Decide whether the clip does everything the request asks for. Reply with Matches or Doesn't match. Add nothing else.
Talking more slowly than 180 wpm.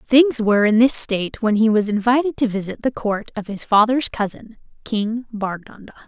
Doesn't match